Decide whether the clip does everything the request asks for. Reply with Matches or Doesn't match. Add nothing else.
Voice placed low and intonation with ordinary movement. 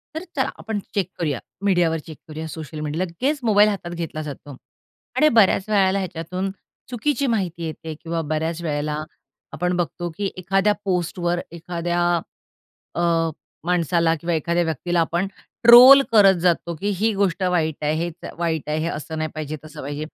Doesn't match